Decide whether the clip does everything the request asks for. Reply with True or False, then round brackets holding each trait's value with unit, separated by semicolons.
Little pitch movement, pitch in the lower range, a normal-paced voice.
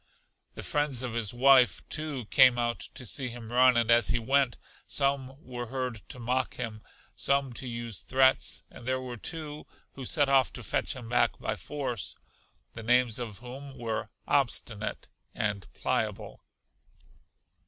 True (2.2 semitones; 125 Hz; 160 wpm)